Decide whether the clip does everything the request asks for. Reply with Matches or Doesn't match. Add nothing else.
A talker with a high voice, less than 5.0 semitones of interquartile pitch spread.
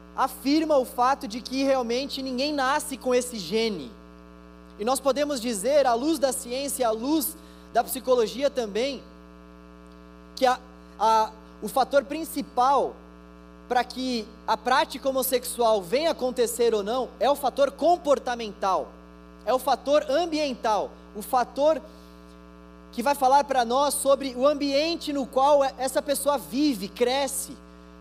Doesn't match